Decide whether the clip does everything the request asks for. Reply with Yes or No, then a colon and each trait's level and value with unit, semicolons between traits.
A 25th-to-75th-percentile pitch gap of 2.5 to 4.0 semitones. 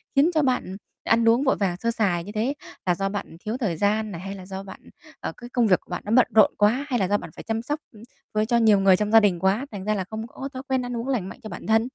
Yes: average, 3.7 semitones